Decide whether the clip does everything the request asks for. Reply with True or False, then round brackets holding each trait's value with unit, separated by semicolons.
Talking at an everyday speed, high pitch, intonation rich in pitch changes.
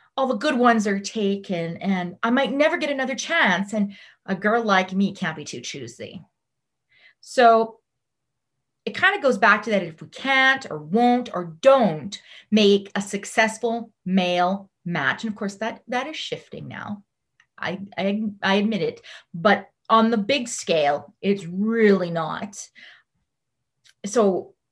False (155 wpm; 210 Hz; 3.9 semitones)